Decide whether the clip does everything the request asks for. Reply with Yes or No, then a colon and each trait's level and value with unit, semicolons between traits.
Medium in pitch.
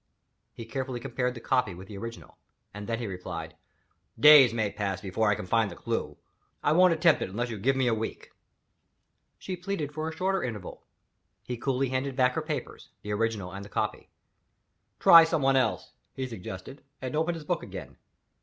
No: low, 125 Hz